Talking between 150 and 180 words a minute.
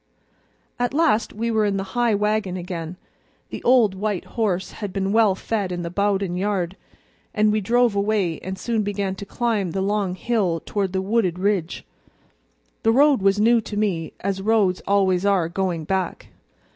Yes: average, 175 wpm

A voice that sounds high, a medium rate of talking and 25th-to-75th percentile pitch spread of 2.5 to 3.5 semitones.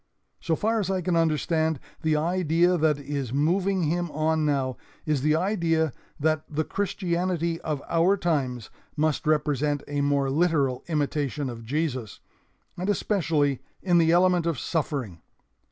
No: medium, 155 Hz; average, 145 wpm; average, 3.2 semitones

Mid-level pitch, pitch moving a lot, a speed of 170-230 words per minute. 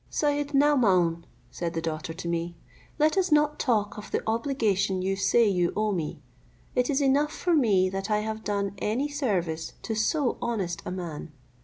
No: high, 210 Hz; wide, 7.4 semitones; average, 180 wpm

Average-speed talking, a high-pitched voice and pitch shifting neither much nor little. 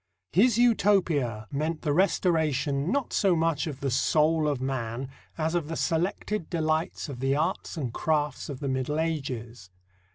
No: average, 160 wpm; medium, 155 Hz; average, 3.5 semitones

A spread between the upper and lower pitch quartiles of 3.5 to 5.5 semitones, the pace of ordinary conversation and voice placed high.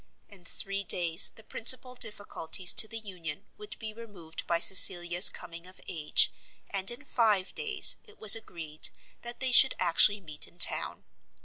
Yes: average, 4.7 semitones; average, 165 wpm; high, 195 Hz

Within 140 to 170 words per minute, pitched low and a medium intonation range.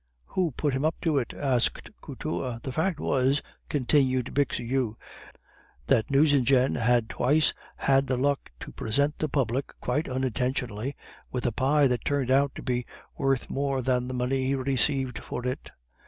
No: average, 160 wpm; low, 130 Hz; narrow, 2.1 semitones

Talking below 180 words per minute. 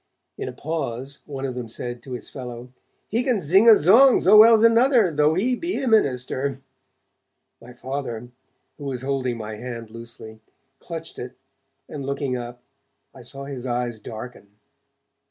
Yes: average, 160 wpm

